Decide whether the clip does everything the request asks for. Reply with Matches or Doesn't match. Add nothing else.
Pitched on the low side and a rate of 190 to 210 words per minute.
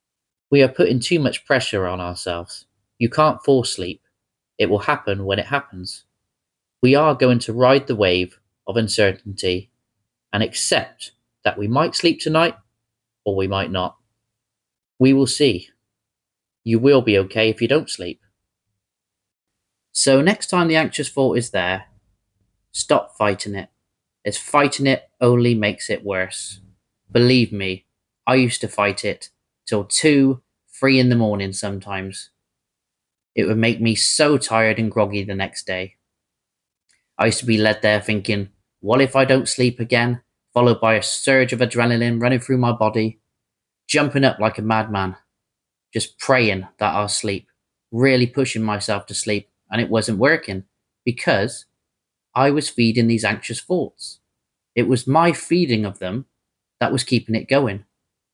Doesn't match